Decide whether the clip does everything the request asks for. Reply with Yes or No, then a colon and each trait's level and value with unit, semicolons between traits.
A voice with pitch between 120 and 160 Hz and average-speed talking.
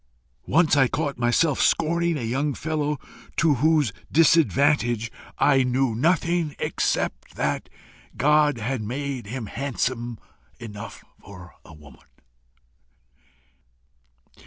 No: low, 135 Hz; slow, 105 wpm